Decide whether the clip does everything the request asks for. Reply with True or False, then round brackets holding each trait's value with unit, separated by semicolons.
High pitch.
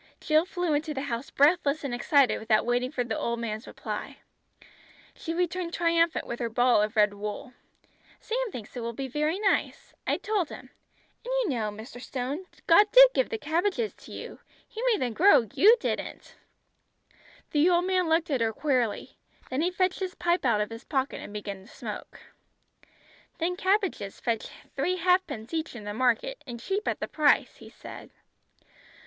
True (295 Hz)